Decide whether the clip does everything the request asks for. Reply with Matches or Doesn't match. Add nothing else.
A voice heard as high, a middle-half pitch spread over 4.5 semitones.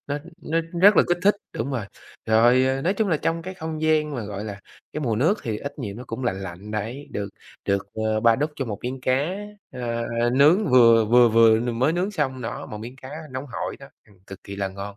Doesn't match